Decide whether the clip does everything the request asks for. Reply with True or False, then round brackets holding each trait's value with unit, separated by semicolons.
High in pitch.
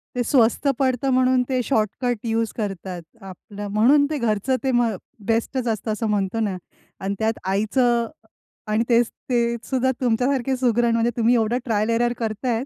True (230 Hz)